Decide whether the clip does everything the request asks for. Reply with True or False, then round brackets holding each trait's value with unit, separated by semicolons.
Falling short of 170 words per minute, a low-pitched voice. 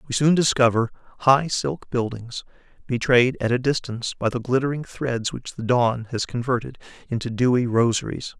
True (155 wpm; 125 Hz)